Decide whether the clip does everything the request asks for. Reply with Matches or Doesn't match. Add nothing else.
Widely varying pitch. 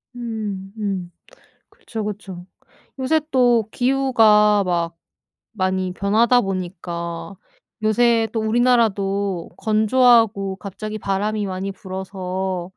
Doesn't match